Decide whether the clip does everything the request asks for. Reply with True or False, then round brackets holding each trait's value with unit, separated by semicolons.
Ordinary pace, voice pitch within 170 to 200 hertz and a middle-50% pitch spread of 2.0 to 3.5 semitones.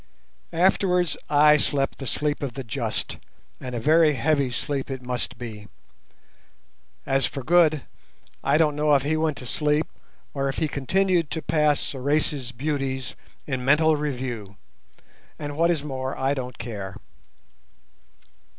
False (145 wpm; 140 Hz; 2.9 semitones)